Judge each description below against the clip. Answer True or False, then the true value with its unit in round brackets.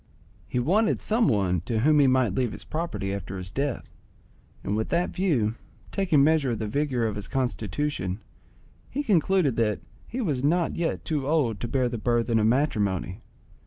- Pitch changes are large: True (6.3 semitones)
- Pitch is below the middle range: True (130 Hz)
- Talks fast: False (180 wpm)